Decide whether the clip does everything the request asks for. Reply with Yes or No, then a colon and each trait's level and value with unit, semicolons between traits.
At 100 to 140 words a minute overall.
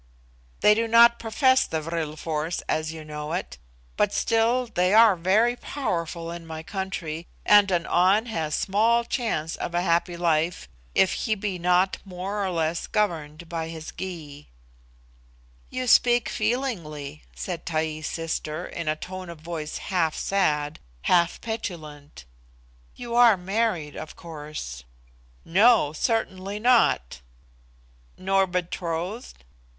Yes: slow, 135 wpm